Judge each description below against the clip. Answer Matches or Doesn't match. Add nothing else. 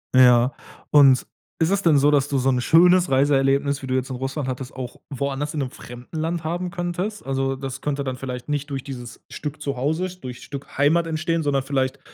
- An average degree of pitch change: Matches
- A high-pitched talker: Doesn't match